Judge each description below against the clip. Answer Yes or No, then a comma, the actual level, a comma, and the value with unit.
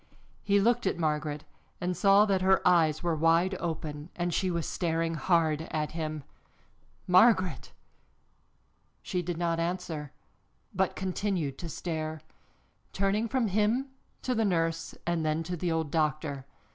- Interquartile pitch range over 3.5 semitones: No, average, 3.2 semitones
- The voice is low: No, medium, 170 Hz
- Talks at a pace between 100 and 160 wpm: Yes, average, 145 wpm